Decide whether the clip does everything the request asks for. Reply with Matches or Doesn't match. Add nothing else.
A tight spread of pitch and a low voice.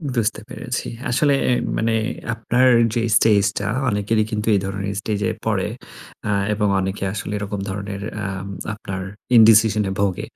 Matches